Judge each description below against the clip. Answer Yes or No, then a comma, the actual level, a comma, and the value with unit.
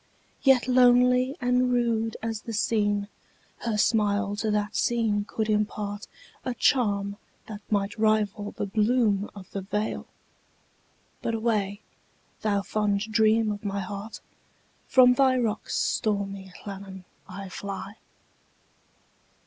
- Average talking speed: No, slow, 110 wpm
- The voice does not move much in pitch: Yes, narrow, 2.2 semitones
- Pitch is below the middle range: No, high, 210 Hz